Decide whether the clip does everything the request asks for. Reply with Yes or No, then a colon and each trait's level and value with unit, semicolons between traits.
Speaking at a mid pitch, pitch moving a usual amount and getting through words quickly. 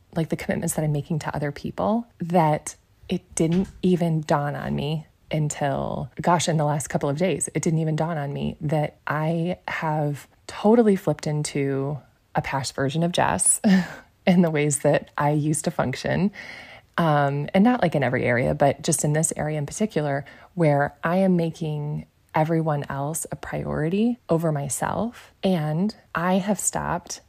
No: medium, 155 Hz; average, 3.5 semitones; average, 170 wpm